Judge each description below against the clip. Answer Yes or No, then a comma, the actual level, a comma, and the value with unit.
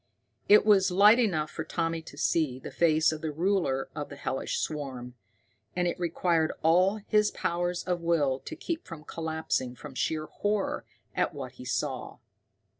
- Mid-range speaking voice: Yes, medium, 165 Hz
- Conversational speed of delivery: Yes, average, 170 wpm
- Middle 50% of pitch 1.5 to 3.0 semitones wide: No, average, 3.4 semitones